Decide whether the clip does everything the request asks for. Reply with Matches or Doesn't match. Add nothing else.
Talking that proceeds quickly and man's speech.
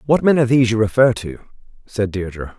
Matches